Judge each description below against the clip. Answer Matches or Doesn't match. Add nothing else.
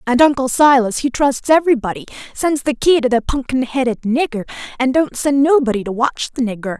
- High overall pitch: Matches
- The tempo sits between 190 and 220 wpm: Matches